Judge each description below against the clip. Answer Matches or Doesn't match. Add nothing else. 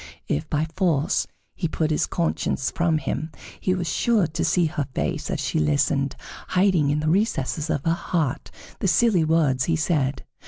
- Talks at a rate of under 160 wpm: Doesn't match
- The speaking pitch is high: Doesn't match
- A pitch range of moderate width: Matches